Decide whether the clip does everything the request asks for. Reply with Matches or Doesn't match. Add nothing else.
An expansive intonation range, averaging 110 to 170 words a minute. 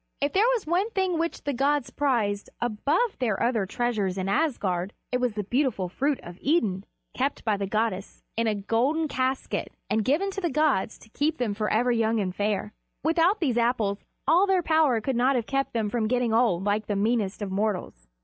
Doesn't match